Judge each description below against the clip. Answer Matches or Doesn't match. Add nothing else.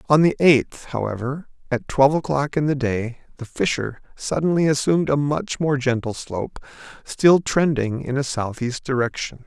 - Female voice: Doesn't match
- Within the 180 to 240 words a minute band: Doesn't match